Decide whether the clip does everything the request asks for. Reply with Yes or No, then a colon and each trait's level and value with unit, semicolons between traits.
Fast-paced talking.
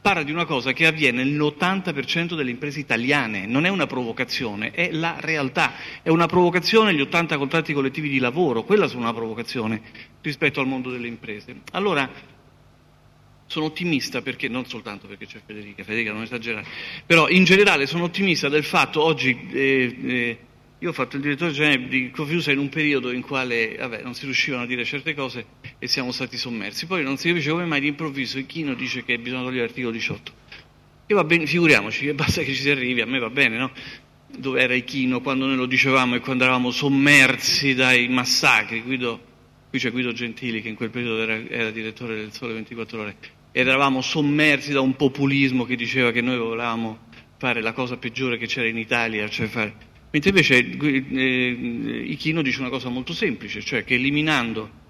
Yes: fast, 185 wpm